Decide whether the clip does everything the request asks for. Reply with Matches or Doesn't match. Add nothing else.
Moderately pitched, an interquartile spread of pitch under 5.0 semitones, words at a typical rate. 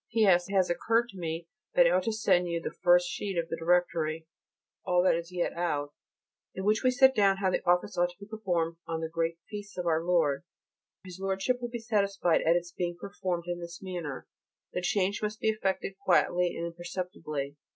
Doesn't match